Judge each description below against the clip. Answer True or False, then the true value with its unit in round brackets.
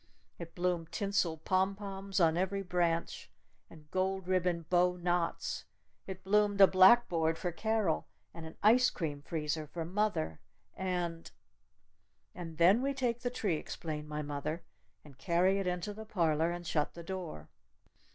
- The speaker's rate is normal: True (150 wpm)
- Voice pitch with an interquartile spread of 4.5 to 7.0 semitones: False (3.1 semitones)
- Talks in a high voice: False (175 Hz)